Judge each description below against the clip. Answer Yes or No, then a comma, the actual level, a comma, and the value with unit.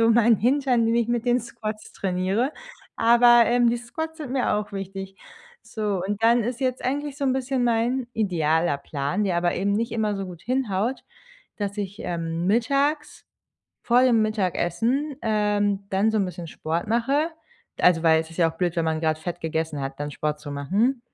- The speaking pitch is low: No, high, 210 Hz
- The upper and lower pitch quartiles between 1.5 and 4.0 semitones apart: No, wide, 5.5 semitones